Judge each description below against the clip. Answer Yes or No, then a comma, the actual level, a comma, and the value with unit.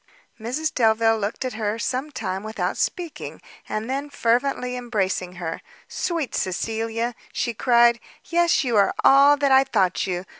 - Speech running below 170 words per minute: Yes, average, 150 wpm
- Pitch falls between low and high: No, high, 235 Hz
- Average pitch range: Yes, average, 3.9 semitones